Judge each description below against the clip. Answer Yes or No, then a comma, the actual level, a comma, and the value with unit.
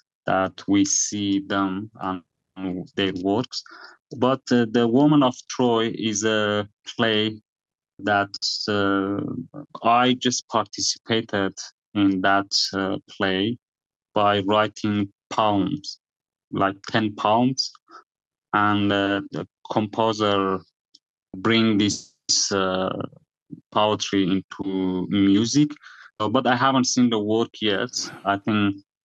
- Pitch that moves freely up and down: No, narrow, 2.5 semitones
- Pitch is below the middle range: Yes, low, 105 Hz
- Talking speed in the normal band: No, slow, 105 wpm